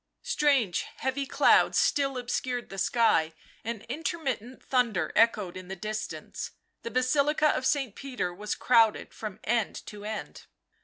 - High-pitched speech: Yes, high, 235 Hz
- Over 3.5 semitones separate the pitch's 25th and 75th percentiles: Yes, average, 4.2 semitones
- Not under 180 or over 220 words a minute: No, average, 140 wpm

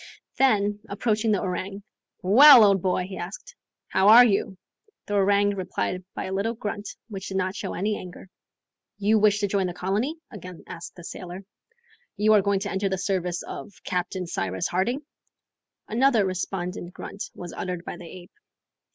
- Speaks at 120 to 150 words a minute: No, average, 170 wpm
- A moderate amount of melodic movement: No, narrow, 2.2 semitones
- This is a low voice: No, high, 195 Hz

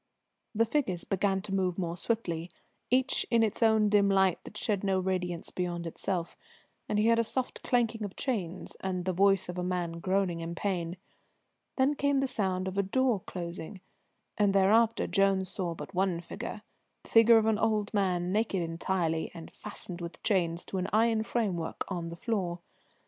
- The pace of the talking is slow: No, average, 180 wpm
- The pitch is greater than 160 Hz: Yes, high, 190 Hz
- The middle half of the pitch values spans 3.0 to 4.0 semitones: Yes, average, 3.7 semitones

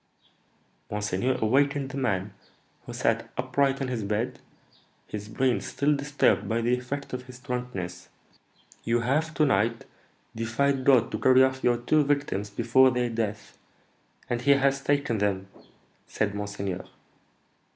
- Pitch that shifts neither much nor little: Yes, average, 4.4 semitones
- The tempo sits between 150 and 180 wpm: No, average, 140 wpm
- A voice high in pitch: No, low, 125 Hz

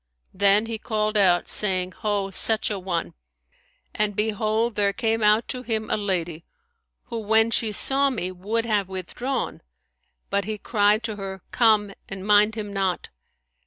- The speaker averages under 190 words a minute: Yes, average, 160 wpm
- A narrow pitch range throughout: Yes, narrow, 2.2 semitones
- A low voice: No, high, 210 Hz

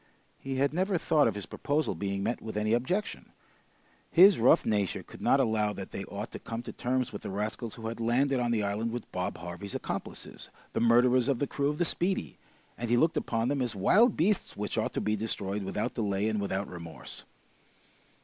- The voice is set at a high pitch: No, low, 115 Hz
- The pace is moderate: No, fast, 210 wpm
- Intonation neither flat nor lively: Yes, average, 4.7 semitones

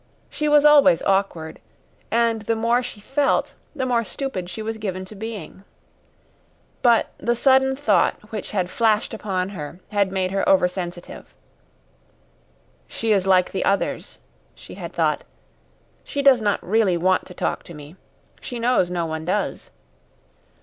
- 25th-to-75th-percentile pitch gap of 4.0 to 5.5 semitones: Yes, average, 4.3 semitones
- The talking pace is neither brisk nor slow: Yes, average, 155 wpm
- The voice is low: No, high, 205 Hz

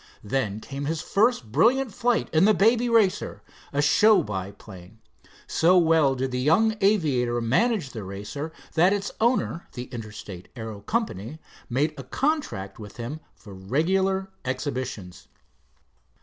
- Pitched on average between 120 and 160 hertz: Yes, medium, 140 Hz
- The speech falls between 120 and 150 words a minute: Yes, slow, 135 wpm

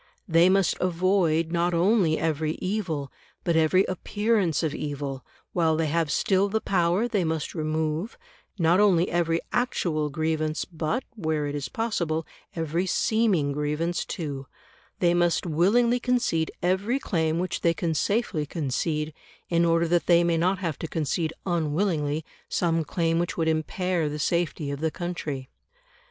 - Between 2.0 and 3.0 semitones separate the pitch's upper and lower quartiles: Yes, average, 2.7 semitones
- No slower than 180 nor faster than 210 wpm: No, average, 150 wpm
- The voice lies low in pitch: No, medium, 165 Hz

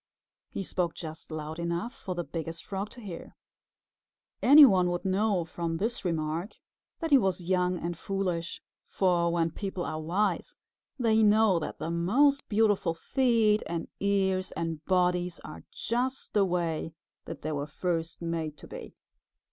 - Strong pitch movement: No, average, 3.7 semitones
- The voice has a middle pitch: Yes, medium, 180 Hz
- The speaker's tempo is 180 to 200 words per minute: No, average, 155 wpm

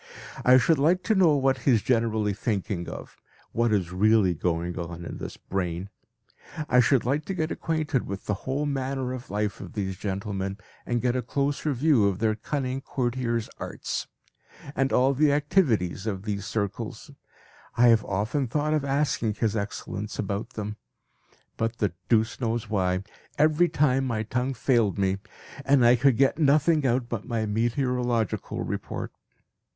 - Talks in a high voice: No, low, 120 Hz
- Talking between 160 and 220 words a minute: Yes, average, 165 wpm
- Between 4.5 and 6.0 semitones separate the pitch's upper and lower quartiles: Yes, average, 4.8 semitones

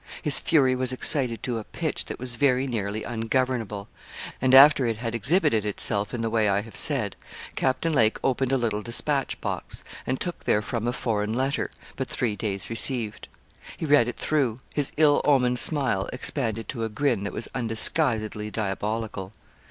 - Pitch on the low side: Yes, low, 120 Hz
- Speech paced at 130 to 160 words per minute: No, average, 175 wpm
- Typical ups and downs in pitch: Yes, average, 3.6 semitones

